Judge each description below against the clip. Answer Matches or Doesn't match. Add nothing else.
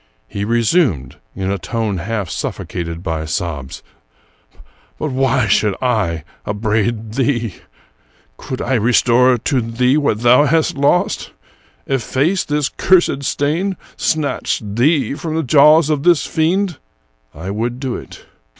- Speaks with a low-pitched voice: Matches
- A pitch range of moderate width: Doesn't match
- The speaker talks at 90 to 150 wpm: Matches